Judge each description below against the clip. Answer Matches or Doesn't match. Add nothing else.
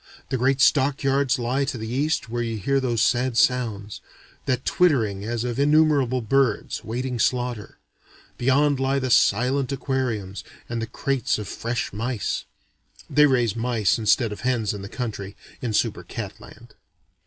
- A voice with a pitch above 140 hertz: Doesn't match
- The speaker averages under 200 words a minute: Matches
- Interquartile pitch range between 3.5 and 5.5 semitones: Doesn't match